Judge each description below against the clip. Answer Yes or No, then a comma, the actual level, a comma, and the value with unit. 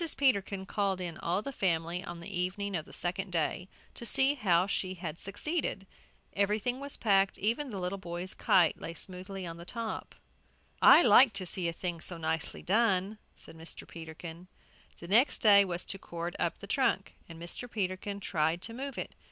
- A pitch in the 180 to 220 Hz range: Yes, high, 190 Hz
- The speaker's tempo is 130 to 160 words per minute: No, average, 185 wpm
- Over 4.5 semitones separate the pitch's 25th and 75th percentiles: No, average, 3.3 semitones